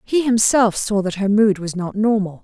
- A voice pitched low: No, high, 210 Hz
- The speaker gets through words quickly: Yes, fast, 220 wpm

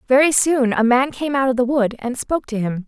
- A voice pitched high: Yes, very high, 255 Hz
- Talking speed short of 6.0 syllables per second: Yes, 5.5 syllables/s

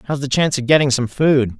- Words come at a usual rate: No, fast, 265 wpm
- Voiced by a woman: No, male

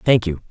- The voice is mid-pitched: No, low, 100 Hz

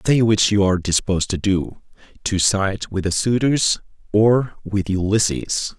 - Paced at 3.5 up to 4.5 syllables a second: Yes, 4.4 syllables/s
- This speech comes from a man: Yes, male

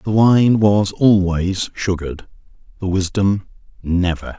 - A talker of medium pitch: No, very low, 95 Hz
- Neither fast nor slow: No, slow, 110 wpm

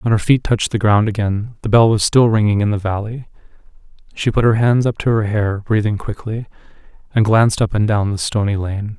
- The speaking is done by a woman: No, male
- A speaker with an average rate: No, fast, 220 wpm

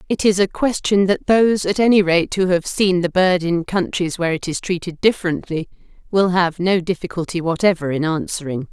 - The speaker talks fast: No, average, 195 wpm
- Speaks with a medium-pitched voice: Yes, medium, 180 Hz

